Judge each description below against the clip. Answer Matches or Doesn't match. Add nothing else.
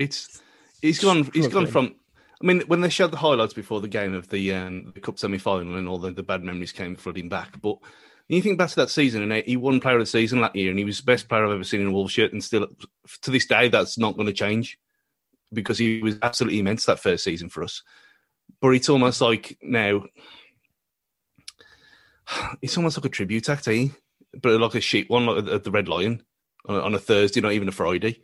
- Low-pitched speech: Matches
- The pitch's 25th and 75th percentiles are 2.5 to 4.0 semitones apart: Doesn't match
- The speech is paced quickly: Matches